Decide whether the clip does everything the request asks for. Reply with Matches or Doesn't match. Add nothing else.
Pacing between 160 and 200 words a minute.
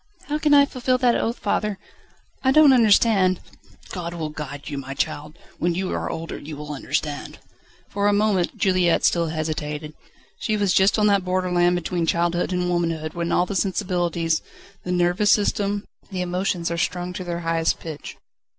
Matches